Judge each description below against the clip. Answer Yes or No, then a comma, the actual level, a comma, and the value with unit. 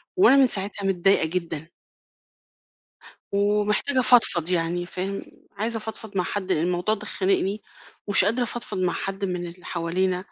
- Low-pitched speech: No, high, 195 Hz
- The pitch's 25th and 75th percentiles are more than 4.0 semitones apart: No, average, 2.8 semitones